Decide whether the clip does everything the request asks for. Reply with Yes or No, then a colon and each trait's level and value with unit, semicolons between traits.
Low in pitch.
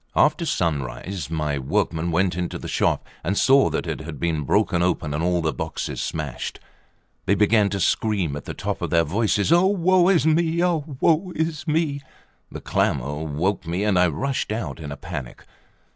Yes: very low, 90 Hz